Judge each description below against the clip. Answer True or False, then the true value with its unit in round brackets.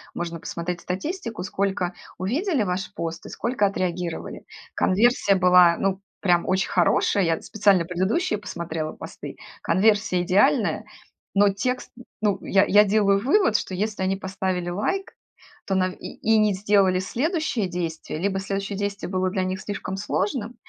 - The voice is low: False (195 Hz)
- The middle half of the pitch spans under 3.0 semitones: True (2.5 semitones)